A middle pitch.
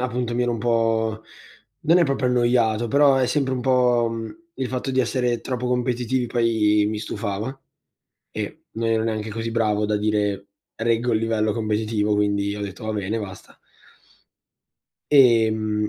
No: low, 115 Hz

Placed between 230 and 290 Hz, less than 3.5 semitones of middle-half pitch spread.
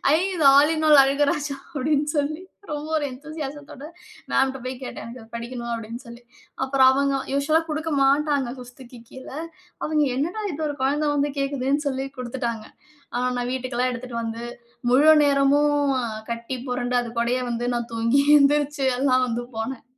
Yes: very high, 270 Hz; average, 3.0 semitones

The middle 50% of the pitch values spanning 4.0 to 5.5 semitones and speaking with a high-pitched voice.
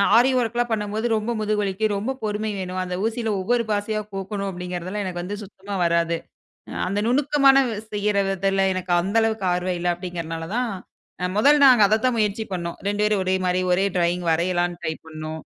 No: average, 3.5 semitones; high, 200 Hz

